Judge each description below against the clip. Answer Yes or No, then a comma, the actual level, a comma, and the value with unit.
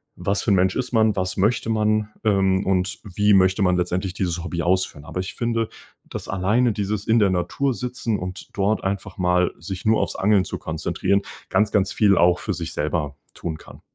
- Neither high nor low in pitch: No, very low, 95 Hz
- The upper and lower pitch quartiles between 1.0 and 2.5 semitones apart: No, average, 2.9 semitones